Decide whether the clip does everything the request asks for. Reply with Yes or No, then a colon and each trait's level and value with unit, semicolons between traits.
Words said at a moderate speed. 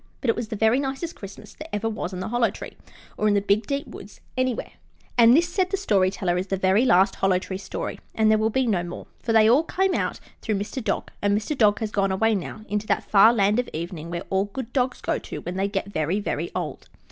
No: fast, 255 wpm